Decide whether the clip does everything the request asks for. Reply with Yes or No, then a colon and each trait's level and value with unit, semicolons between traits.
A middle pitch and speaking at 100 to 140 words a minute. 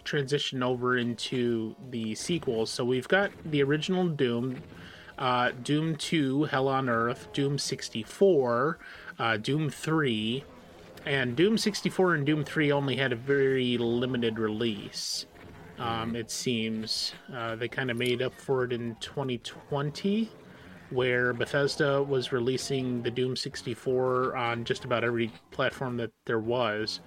No: low, 125 Hz; slow, 135 wpm